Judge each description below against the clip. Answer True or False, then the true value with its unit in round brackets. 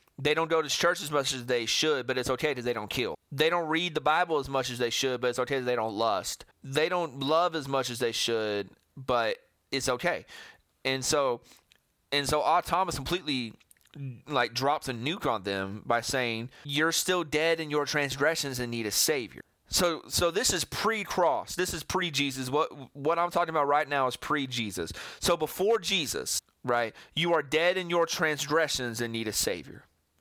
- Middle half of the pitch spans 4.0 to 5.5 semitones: True (4.6 semitones)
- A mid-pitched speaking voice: True (145 Hz)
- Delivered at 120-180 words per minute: False (200 wpm)